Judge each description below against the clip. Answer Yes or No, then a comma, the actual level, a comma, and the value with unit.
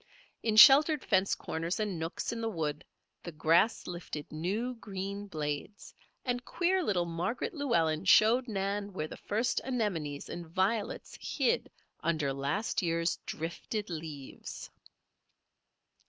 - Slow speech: Yes, slow, 125 wpm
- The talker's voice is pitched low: No, high, 190 Hz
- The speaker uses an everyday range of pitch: No, wide, 5.7 semitones